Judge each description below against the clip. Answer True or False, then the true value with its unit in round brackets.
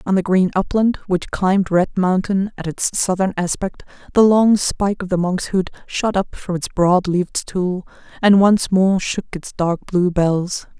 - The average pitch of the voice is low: False (185 Hz)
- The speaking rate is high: False (185 wpm)